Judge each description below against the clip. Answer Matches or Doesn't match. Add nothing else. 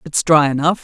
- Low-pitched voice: Doesn't match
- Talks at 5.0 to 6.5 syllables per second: Matches